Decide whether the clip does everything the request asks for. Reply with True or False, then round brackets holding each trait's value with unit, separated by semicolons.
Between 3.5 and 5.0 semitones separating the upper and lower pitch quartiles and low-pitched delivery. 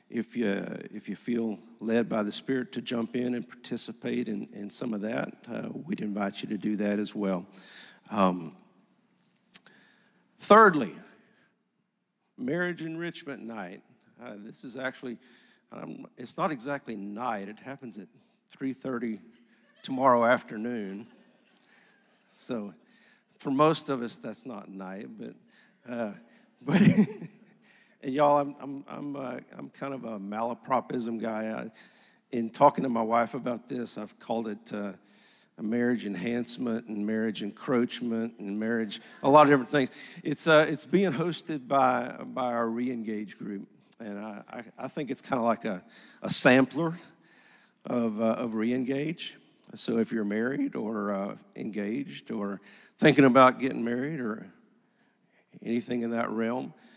True (4.3 semitones; 120 Hz)